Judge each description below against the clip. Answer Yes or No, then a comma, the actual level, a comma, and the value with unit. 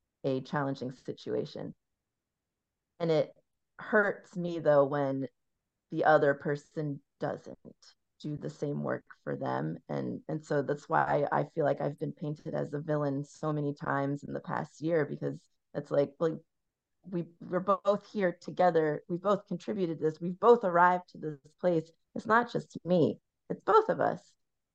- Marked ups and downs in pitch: No, average, 3.8 semitones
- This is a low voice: No, medium, 155 Hz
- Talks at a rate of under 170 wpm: Yes, average, 160 wpm